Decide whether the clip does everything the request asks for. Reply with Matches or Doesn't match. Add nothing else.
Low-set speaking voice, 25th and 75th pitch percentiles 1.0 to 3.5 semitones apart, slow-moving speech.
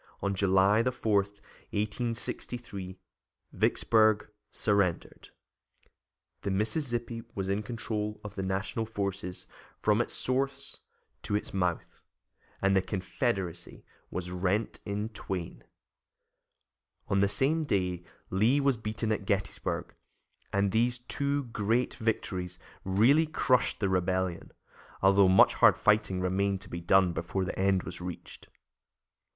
Matches